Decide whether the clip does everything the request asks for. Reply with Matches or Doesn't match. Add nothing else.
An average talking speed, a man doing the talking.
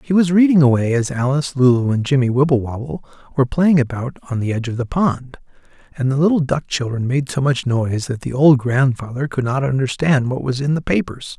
Doesn't match